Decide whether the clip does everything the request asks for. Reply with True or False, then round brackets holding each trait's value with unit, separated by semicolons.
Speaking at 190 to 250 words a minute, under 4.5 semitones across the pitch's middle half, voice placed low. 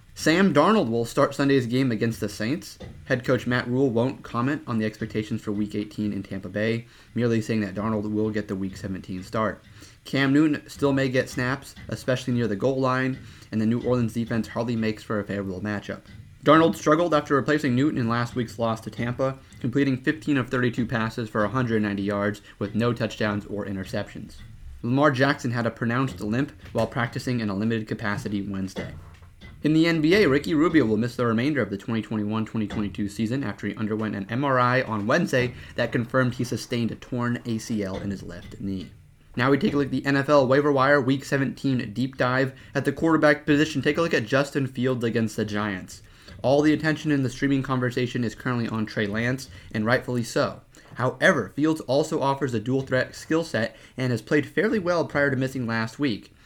True (200 wpm; 4.0 semitones; 120 Hz)